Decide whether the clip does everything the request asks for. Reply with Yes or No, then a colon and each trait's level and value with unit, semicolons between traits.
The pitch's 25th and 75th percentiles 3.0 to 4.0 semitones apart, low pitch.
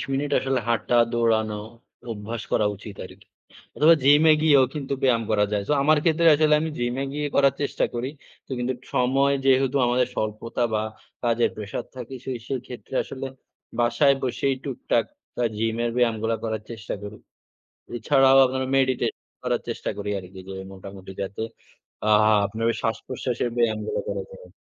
Yes: average, 3.7 semitones; low, 120 Hz